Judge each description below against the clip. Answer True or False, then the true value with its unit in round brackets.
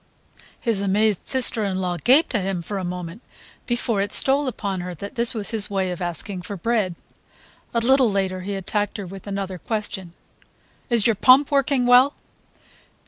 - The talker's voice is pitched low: False (205 Hz)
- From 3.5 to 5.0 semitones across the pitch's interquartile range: True (4.1 semitones)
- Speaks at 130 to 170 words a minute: False (180 wpm)